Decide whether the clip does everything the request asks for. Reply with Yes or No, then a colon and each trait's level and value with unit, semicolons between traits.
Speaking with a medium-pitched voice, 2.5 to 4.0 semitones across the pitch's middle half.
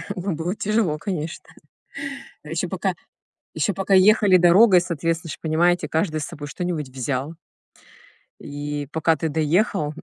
Yes: medium, 165 Hz; average, 3.5 semitones